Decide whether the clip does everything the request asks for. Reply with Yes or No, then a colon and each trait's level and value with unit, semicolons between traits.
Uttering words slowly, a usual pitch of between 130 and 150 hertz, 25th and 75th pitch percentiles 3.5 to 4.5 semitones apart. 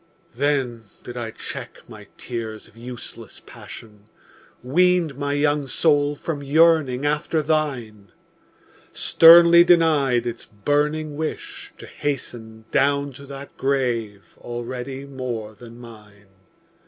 Yes: slow, 115 wpm; low, 135 Hz; average, 4.0 semitones